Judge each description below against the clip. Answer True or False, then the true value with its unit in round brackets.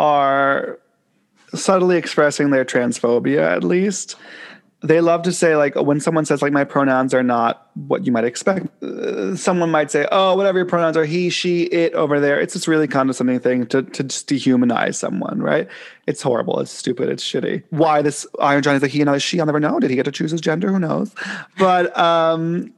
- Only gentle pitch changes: False (4.1 semitones)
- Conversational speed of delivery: False (210 wpm)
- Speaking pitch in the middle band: True (160 Hz)